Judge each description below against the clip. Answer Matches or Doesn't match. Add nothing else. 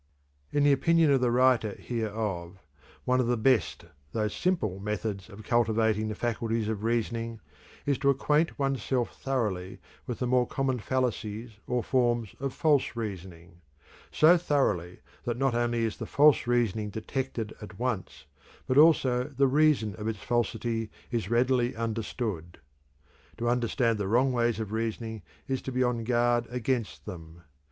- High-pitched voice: Doesn't match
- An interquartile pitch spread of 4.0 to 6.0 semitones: Doesn't match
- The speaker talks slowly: Doesn't match